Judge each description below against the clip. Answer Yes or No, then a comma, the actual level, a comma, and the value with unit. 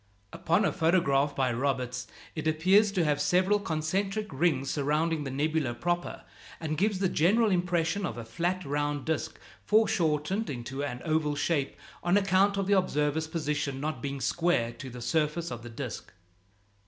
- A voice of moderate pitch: Yes, medium, 155 Hz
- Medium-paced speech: Yes, average, 165 wpm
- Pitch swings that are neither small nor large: Yes, average, 4.4 semitones